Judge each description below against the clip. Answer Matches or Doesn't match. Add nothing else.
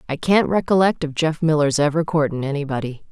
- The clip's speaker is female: Matches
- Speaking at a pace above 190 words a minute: Doesn't match